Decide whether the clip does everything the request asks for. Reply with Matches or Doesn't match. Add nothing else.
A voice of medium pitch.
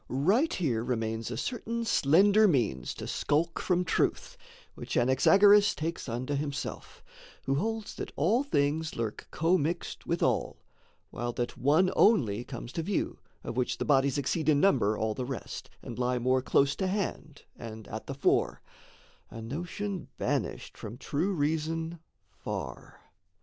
Matches